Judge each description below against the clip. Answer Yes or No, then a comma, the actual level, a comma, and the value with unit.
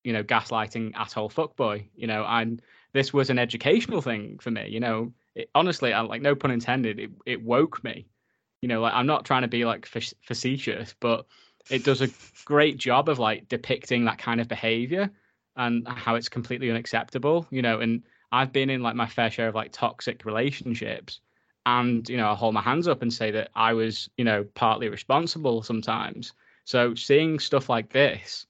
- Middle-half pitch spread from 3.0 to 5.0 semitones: No, narrow, 2.4 semitones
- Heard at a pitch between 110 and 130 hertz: Yes, low, 120 Hz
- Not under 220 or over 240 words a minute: No, average, 200 wpm